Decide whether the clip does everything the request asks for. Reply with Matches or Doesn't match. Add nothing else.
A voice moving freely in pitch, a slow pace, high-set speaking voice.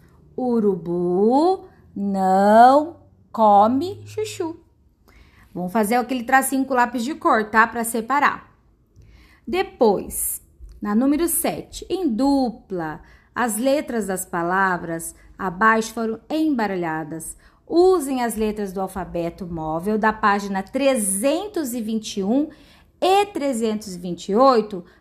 Matches